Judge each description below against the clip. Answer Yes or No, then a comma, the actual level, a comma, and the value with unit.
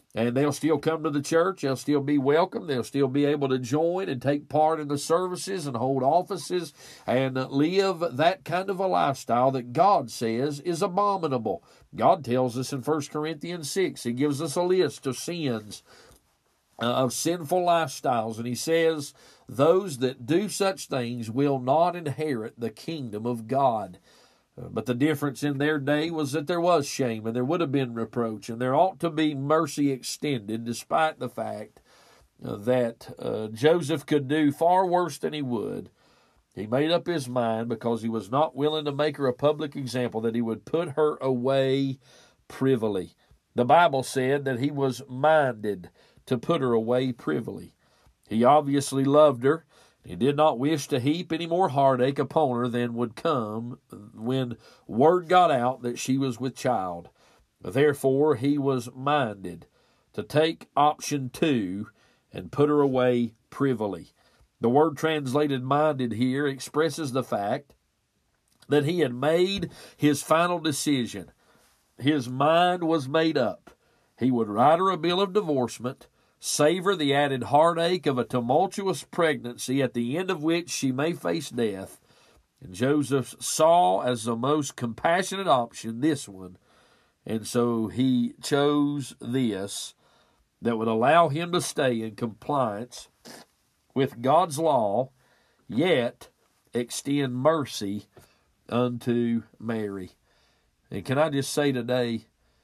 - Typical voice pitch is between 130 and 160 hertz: Yes, medium, 140 Hz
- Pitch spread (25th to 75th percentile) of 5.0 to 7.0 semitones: No, average, 4.4 semitones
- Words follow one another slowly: No, average, 155 wpm